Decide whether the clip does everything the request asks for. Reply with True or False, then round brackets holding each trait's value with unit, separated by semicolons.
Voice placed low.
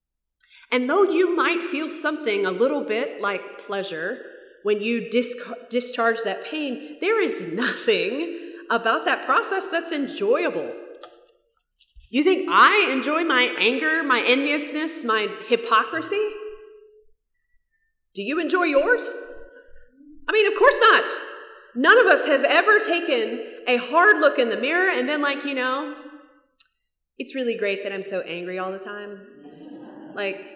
False (305 Hz)